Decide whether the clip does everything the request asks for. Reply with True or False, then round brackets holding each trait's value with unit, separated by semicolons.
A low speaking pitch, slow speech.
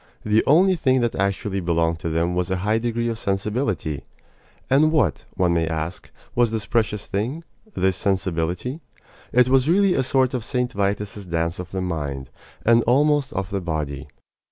False (100 Hz; 175 wpm)